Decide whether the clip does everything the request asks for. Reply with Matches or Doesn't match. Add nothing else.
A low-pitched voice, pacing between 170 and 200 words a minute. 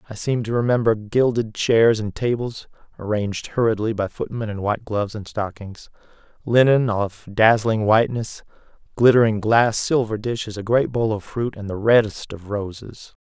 Doesn't match